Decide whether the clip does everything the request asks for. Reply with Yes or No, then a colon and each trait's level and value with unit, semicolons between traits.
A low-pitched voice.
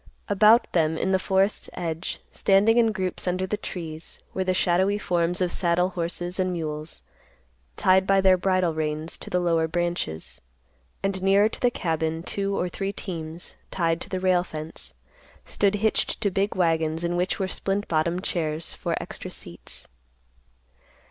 No: medium, 180 Hz